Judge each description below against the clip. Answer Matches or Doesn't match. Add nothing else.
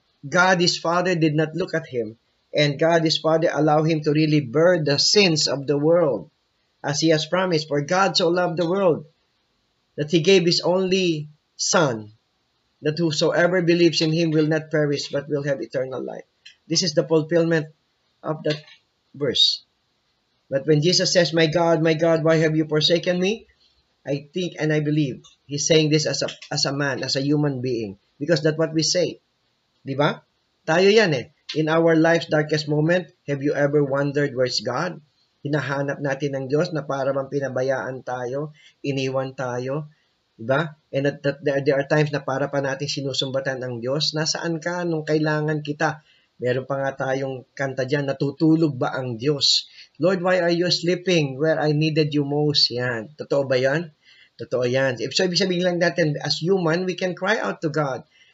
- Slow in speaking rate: Doesn't match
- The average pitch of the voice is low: Doesn't match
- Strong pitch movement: Doesn't match